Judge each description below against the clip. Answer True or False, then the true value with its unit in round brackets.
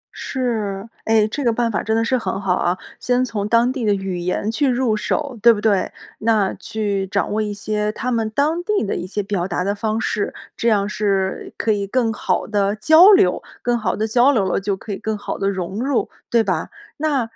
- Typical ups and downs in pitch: True (3.1 semitones)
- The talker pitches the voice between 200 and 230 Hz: True (215 Hz)